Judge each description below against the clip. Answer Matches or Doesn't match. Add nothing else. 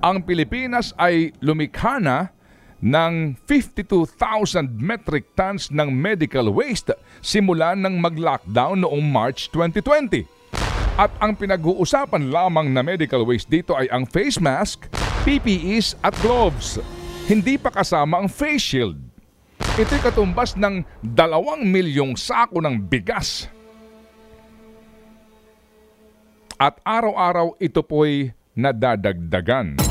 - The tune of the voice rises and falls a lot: Matches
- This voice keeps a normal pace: Doesn't match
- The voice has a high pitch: Doesn't match